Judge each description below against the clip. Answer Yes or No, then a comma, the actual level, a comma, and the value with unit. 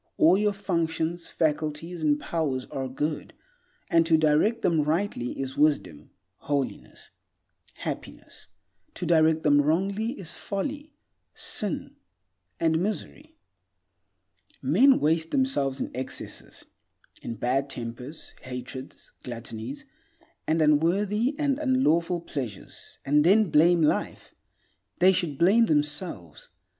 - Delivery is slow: Yes, slow, 110 wpm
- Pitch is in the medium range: Yes, medium, 160 Hz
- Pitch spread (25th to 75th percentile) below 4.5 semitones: No, average, 5.2 semitones